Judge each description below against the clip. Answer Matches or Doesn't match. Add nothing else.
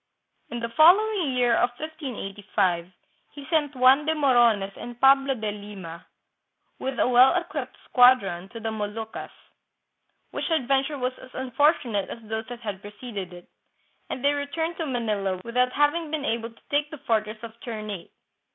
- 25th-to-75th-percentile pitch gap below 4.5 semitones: Doesn't match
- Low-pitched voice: Doesn't match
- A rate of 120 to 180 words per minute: Matches